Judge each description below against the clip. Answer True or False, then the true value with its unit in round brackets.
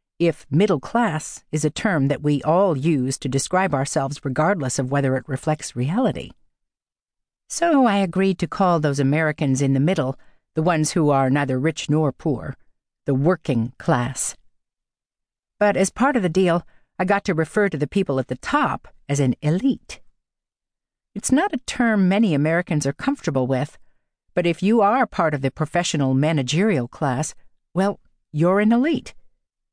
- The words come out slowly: False (165 wpm)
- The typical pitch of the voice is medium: True (155 Hz)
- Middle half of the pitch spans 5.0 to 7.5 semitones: True (5.5 semitones)